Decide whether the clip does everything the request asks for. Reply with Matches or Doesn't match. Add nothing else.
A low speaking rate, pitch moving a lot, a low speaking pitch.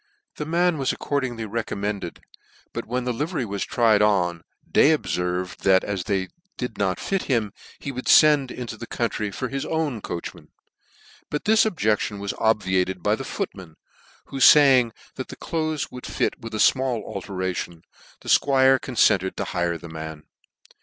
Doesn't match